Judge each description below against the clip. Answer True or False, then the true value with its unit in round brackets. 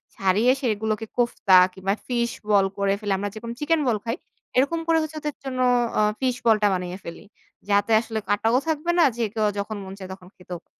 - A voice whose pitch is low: False (220 Hz)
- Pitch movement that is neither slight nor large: True (4.2 semitones)